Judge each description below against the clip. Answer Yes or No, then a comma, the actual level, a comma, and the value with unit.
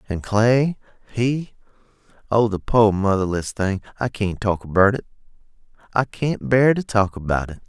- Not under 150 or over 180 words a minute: No, slow, 135 wpm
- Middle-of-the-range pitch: No, low, 110 Hz